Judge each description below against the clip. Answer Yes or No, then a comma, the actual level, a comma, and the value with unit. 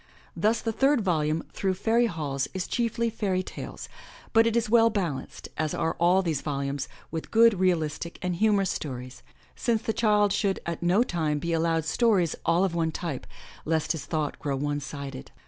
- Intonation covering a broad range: Yes, wide, 5.8 semitones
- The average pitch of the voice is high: No, medium, 175 Hz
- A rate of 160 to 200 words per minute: Yes, average, 180 wpm